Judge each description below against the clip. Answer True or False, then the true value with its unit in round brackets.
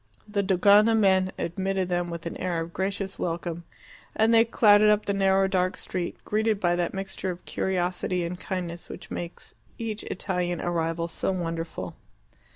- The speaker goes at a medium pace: True (160 wpm)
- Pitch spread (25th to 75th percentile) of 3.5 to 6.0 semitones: False (2.4 semitones)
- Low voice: False (185 Hz)